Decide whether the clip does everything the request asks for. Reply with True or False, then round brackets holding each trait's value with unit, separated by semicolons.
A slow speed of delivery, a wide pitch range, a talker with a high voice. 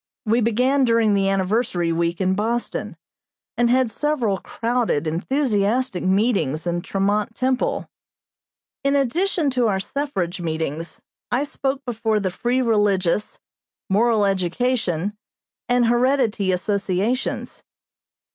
False (110 wpm; 4.8 semitones; 220 Hz)